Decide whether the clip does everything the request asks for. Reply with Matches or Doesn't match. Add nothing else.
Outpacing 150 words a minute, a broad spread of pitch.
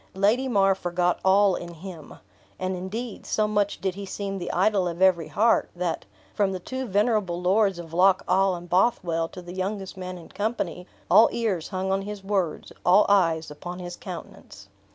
Doesn't match